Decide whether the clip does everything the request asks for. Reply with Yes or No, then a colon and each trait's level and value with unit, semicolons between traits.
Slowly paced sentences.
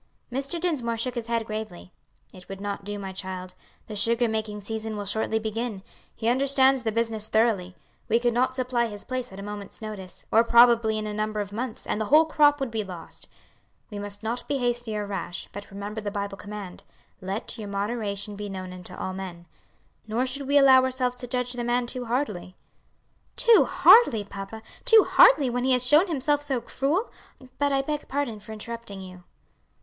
No: average, 195 wpm